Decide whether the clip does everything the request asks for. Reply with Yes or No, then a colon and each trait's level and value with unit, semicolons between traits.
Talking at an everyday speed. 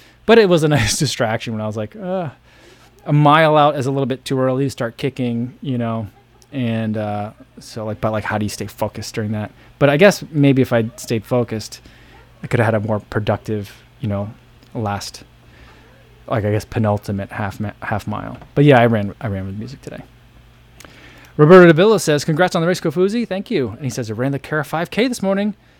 No: fast, 220 wpm